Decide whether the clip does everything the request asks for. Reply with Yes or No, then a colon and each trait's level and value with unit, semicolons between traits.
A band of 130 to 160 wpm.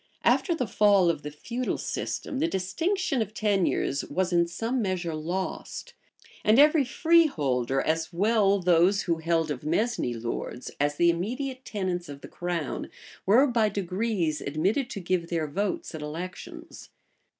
Yes: average, 150 wpm